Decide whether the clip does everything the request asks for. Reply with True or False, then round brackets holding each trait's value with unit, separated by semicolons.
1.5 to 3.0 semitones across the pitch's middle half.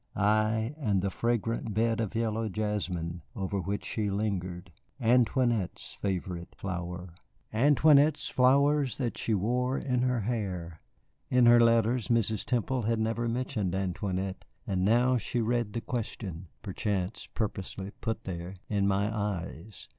False (3.8 semitones)